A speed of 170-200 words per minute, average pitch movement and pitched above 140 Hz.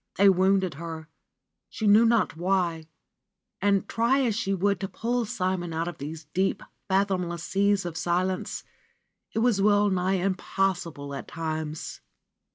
No: average, 145 wpm; average, 3.1 semitones; high, 190 Hz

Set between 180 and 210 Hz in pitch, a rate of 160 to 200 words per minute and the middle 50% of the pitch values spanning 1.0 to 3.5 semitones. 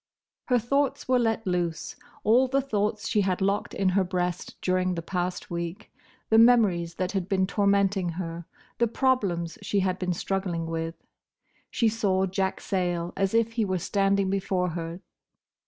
Yes: high, 190 Hz; average, 165 wpm; average, 3.2 semitones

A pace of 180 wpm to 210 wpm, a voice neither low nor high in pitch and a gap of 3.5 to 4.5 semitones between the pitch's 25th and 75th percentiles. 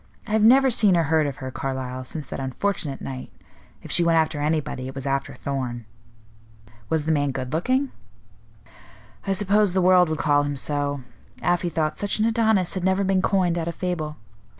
No: average, 195 wpm; medium, 160 Hz; average, 5.2 semitones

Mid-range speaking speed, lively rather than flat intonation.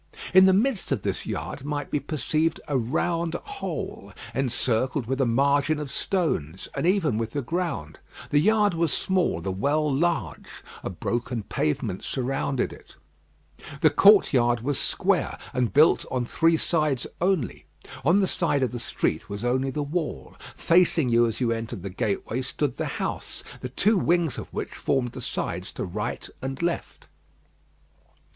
Yes: average, 165 wpm; wide, 5.9 semitones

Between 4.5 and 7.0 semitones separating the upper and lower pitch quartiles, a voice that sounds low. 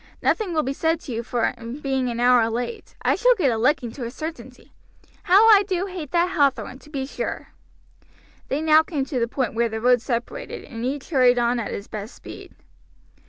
No: average, 5.0 semitones; very high, 265 Hz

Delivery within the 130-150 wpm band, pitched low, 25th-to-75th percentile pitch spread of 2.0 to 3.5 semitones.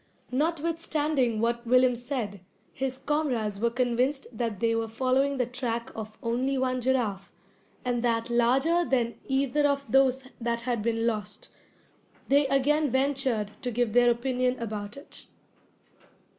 No: average, 140 wpm; very high, 250 Hz; average, 2.7 semitones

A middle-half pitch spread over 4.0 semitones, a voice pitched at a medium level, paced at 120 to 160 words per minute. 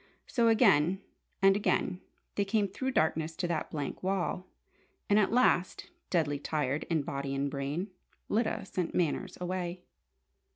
Yes: average, 4.5 semitones; medium, 180 Hz; average, 140 wpm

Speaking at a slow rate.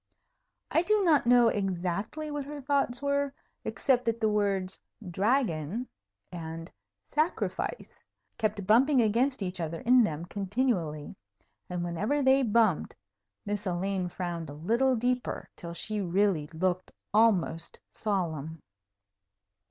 Yes: slow, 120 wpm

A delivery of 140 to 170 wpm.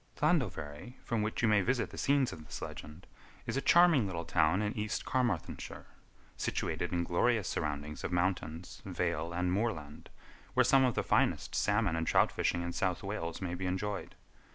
No: average, 180 wpm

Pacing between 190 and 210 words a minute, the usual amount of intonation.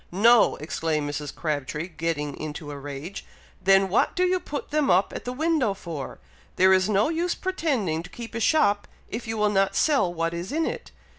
No: average, 200 wpm; wide, 7.3 semitones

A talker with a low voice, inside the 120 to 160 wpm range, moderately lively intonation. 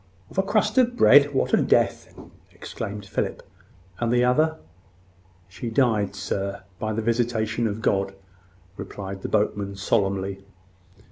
Yes: low, 110 Hz; slow, 135 wpm; average, 4.1 semitones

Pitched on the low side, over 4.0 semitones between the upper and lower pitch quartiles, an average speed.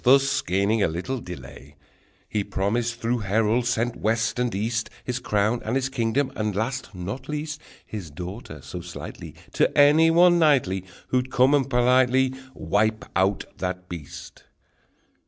Yes: low, 115 Hz; average, 4.9 semitones; average, 150 wpm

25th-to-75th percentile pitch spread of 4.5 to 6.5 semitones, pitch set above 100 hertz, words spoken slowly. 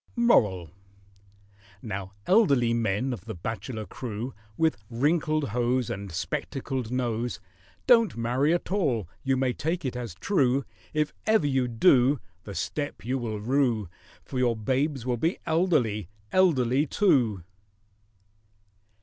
Yes: average, 4.8 semitones; low, 125 Hz; slow, 125 wpm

